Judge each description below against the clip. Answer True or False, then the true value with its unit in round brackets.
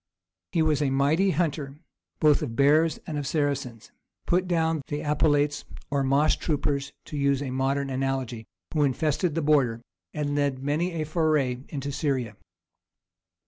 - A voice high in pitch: False (145 Hz)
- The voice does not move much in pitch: True (2.3 semitones)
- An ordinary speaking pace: True (150 wpm)